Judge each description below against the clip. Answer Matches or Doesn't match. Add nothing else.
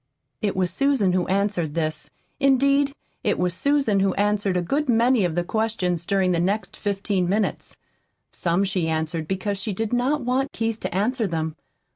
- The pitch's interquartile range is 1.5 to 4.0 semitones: Doesn't match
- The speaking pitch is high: Matches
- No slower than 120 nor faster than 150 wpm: Doesn't match